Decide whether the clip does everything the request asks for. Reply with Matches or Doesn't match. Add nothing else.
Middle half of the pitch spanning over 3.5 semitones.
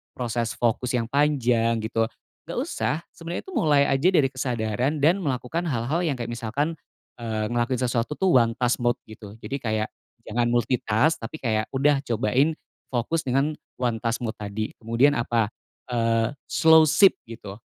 Matches